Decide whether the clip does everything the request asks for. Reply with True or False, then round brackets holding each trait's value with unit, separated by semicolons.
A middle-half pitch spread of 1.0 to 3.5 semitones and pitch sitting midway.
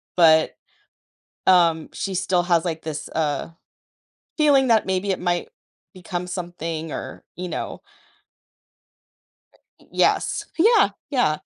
True (2.8 semitones; 175 Hz)